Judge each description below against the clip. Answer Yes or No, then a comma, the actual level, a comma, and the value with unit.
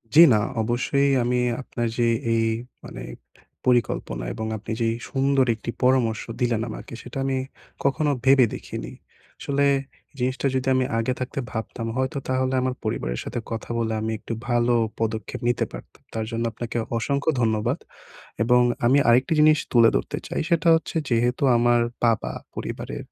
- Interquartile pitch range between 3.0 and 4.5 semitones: No, narrow, 2.5 semitones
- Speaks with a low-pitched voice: Yes, low, 120 Hz